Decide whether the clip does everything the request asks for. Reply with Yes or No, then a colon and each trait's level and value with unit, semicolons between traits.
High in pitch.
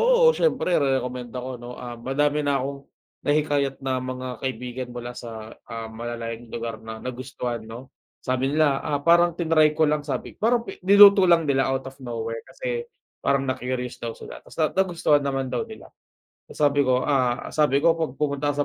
No: low, 135 Hz